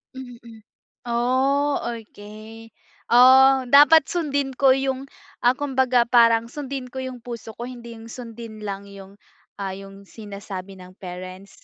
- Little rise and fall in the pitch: No, average, 3.9 semitones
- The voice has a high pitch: Yes, high, 235 Hz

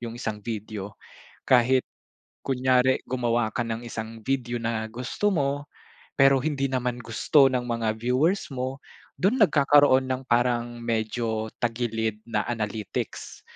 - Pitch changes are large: No, narrow, 2.6 semitones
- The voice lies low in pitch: Yes, low, 120 Hz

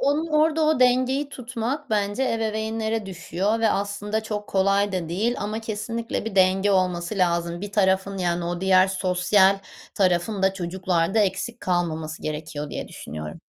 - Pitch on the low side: No, high, 195 Hz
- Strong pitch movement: No, average, 3.6 semitones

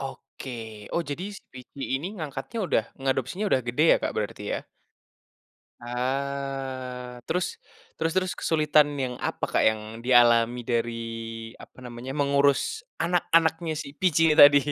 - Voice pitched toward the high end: No, low, 135 Hz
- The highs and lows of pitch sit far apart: No, average, 4.3 semitones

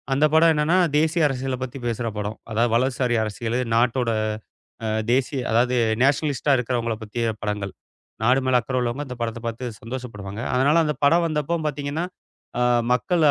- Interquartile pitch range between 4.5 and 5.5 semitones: No, average, 3.7 semitones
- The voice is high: No, low, 125 Hz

